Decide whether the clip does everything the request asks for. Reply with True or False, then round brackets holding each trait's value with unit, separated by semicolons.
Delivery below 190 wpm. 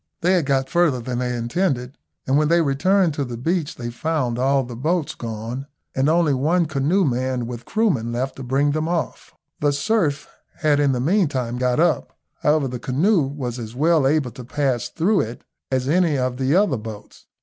False (195 wpm)